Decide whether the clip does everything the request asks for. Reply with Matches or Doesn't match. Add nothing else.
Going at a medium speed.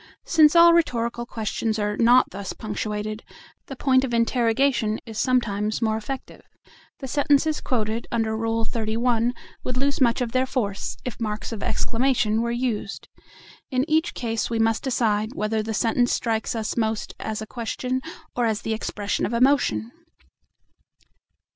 Matches